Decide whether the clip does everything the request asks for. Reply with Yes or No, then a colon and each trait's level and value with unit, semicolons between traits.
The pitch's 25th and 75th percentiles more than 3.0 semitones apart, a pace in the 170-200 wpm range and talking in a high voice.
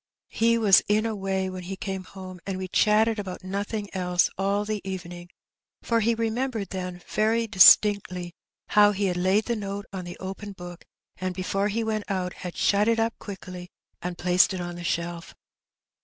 No: narrow, 2.6 semitones; average, 185 wpm; high, 195 Hz